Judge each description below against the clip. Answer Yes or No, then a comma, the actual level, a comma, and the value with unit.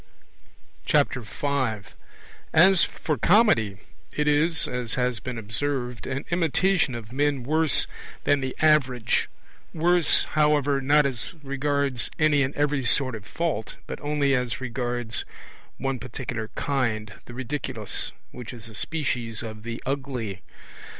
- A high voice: No, low, 130 Hz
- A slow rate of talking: Yes, slow, 130 wpm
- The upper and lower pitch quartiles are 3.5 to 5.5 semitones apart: Yes, average, 3.8 semitones